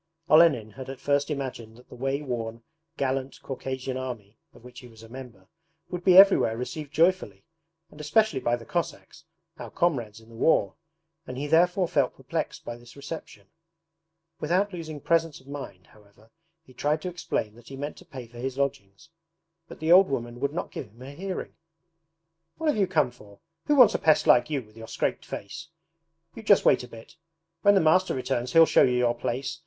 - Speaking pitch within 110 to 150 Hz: Yes, low, 135 Hz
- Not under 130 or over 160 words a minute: No, average, 200 wpm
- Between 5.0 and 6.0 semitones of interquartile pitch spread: Yes, average, 5.3 semitones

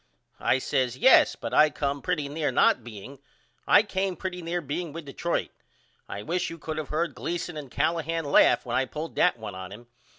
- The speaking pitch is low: No, medium, 150 Hz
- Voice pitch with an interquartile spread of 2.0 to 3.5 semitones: No, average, 4.3 semitones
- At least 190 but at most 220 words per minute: Yes, average, 200 wpm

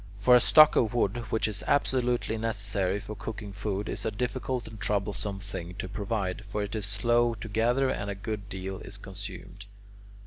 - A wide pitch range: No, average, 2.9 semitones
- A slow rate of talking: No, average, 185 wpm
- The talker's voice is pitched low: Yes, low, 105 Hz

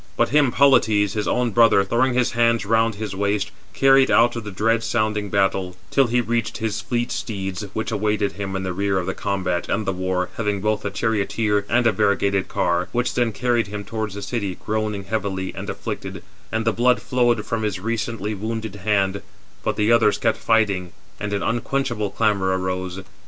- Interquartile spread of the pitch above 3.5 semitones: No, average, 2.7 semitones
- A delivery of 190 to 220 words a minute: Yes, average, 195 wpm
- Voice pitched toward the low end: Yes, low, 105 Hz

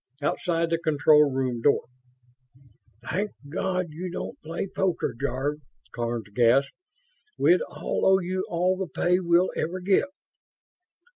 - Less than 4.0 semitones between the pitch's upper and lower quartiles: No, average, 4.6 semitones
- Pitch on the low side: No, medium, 165 Hz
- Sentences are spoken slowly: Yes, slow, 130 wpm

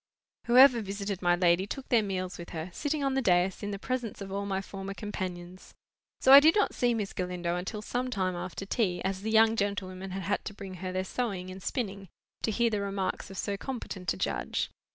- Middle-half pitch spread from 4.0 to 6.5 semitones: No, average, 3.3 semitones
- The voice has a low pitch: No, high, 195 Hz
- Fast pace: Yes, fast, 220 wpm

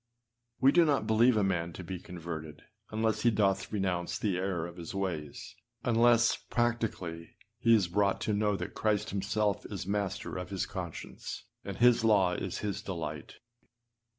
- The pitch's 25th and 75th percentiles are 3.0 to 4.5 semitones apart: Yes, average, 3.5 semitones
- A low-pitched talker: Yes, low, 100 Hz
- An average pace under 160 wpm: No, average, 165 wpm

